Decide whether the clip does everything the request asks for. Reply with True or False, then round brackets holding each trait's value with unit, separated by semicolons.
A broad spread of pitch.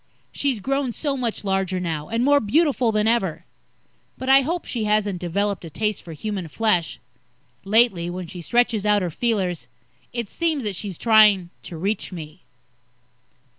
False (4.8 semitones)